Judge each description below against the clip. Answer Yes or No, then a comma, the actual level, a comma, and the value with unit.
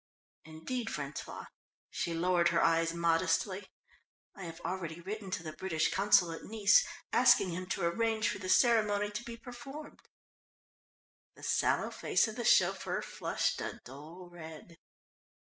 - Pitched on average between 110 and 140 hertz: No, medium, 185 Hz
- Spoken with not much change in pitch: No, average, 4.6 semitones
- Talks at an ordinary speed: Yes, average, 145 wpm